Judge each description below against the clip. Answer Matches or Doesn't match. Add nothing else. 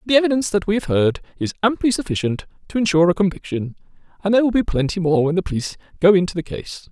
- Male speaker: Matches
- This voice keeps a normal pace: Doesn't match